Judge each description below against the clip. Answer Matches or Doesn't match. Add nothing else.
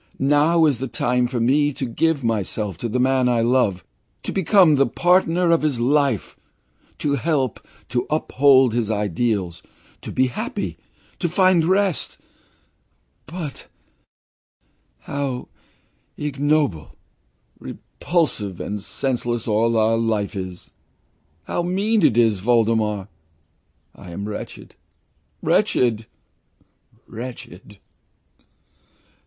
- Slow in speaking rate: Matches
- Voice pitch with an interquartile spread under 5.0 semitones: Doesn't match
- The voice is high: Doesn't match